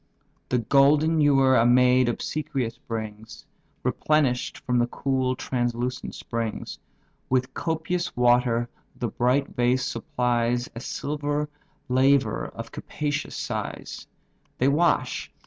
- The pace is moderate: No, slow, 110 wpm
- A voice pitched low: Yes, low, 125 Hz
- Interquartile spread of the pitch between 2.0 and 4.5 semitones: Yes, average, 2.8 semitones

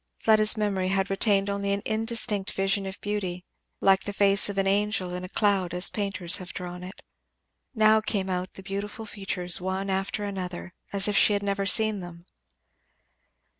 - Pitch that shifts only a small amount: Yes, narrow, 1.7 semitones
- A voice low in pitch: No, high, 195 Hz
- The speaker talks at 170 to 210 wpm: Yes, average, 175 wpm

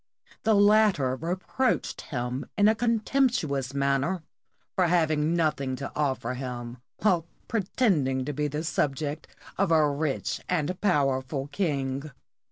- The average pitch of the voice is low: No, medium, 150 Hz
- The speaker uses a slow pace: Yes, slow, 130 wpm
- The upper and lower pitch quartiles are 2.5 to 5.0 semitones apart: No, wide, 5.5 semitones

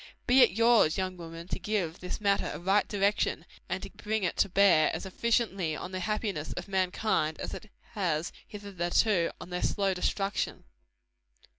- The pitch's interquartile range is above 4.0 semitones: No, average, 3.2 semitones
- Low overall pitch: No, high, 190 Hz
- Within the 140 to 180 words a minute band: Yes, average, 170 wpm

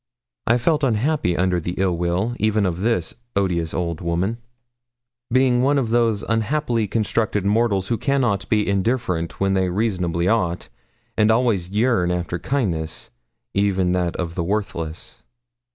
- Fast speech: No, average, 145 wpm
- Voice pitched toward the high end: No, low, 100 Hz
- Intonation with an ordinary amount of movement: Yes, average, 4.7 semitones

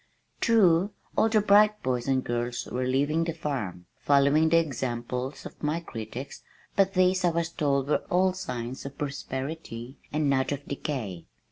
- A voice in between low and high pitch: Yes, medium, 145 Hz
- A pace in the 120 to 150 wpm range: No, average, 160 wpm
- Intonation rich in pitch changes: No, average, 4.7 semitones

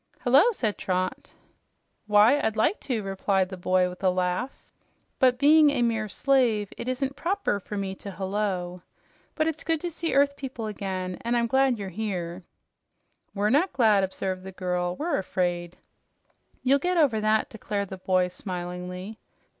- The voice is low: No, high, 210 Hz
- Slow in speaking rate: No, average, 165 wpm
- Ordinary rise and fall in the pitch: No, wide, 6.0 semitones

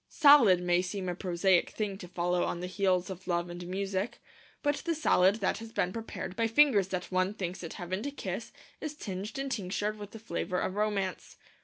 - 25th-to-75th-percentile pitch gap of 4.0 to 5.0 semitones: No, average, 3.2 semitones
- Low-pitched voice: No, high, 190 Hz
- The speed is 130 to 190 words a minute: No, fast, 205 wpm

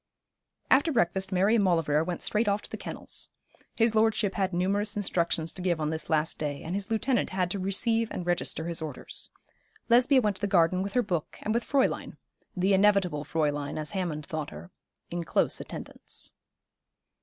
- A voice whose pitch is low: No, medium, 185 Hz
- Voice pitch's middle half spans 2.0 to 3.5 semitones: No, average, 4.3 semitones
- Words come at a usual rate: Yes, average, 185 wpm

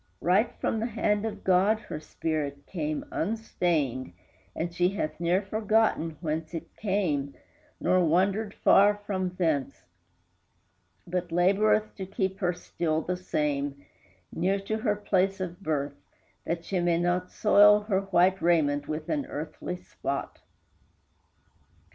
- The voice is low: No, medium, 180 Hz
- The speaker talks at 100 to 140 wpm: Yes, slow, 135 wpm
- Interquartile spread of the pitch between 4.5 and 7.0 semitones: No, average, 4.1 semitones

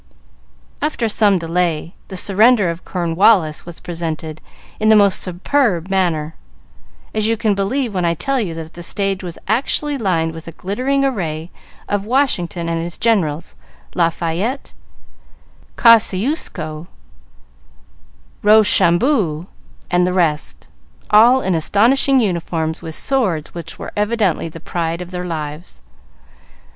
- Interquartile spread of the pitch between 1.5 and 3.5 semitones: No, average, 4.8 semitones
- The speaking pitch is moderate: Yes, medium, 180 Hz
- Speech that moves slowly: Yes, slow, 130 wpm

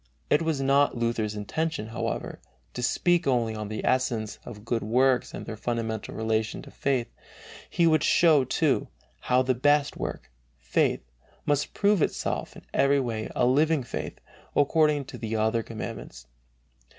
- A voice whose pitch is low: Yes, low, 125 Hz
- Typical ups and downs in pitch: Yes, average, 4.5 semitones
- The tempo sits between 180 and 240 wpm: No, average, 155 wpm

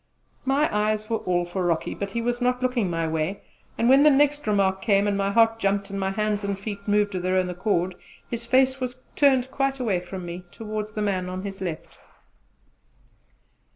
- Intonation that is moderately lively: Yes, average, 4.2 semitones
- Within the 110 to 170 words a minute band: No, fast, 205 wpm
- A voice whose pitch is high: Yes, high, 205 Hz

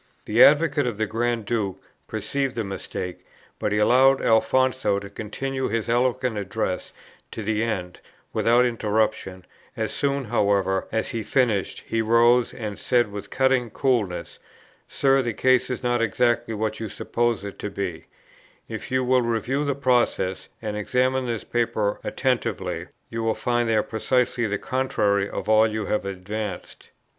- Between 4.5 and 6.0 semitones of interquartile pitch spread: No, average, 3.3 semitones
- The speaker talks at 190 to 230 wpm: No, average, 160 wpm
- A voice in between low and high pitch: No, low, 115 Hz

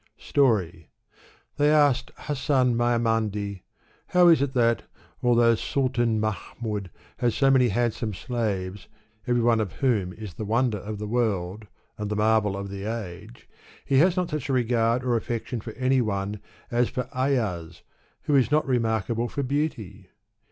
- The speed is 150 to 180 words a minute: Yes, average, 160 wpm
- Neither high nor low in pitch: No, low, 115 Hz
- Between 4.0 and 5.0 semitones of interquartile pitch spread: No, average, 3.5 semitones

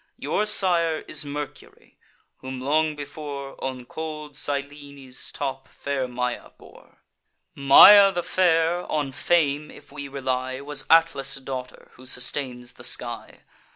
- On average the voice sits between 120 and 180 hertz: Yes, medium, 140 Hz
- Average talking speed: No, slow, 125 wpm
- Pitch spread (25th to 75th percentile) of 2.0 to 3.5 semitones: Yes, average, 2.9 semitones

